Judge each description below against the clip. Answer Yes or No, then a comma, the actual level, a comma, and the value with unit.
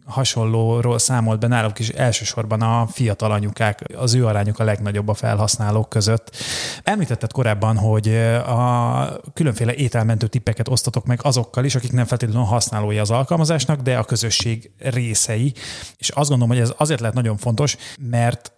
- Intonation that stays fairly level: Yes, narrow, 2.2 semitones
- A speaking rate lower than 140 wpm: No, fast, 155 wpm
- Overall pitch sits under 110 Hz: No, low, 120 Hz